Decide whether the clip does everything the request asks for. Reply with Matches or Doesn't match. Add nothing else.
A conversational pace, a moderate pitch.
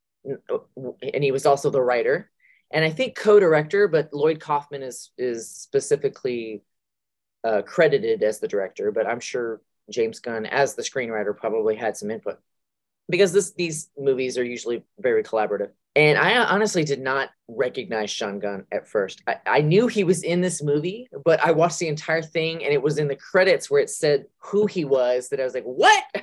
Matches